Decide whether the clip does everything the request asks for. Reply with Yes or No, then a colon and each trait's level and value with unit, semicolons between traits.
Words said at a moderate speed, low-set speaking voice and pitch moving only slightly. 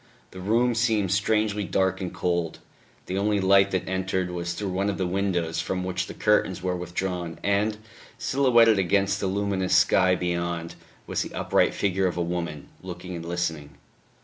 Yes: average, 175 wpm; very low, 95 Hz; narrow, 2.2 semitones